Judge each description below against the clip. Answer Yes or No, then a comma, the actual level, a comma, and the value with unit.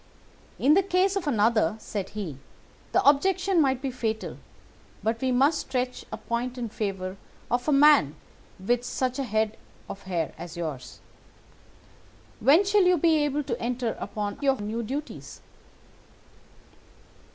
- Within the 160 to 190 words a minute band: No, average, 145 wpm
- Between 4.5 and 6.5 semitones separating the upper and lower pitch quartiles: Yes, wide, 5.5 semitones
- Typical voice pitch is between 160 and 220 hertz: No, high, 245 Hz